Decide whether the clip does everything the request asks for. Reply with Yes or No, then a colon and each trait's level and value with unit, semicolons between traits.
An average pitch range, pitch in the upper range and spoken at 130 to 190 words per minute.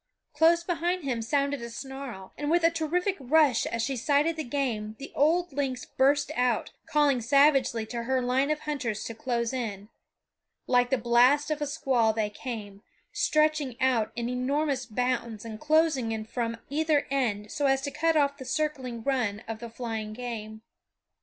Yes: average, 4.1 semitones; very high, 260 Hz; average, 175 wpm